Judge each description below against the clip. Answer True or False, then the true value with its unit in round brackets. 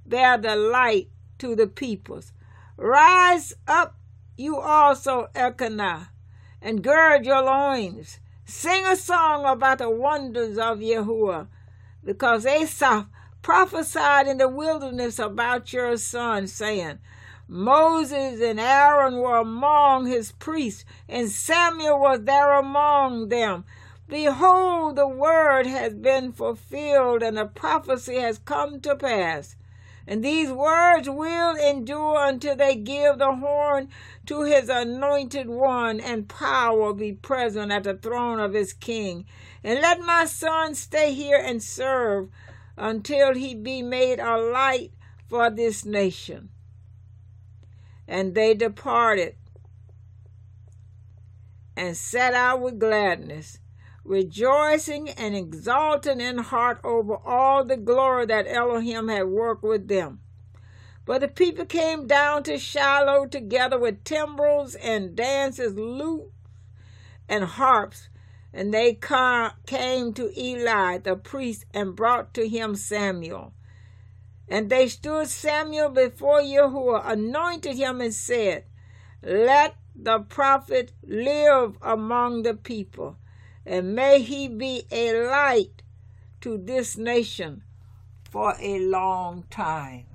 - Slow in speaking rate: True (120 wpm)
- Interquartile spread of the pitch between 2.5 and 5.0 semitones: False (5.6 semitones)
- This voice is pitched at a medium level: False (245 Hz)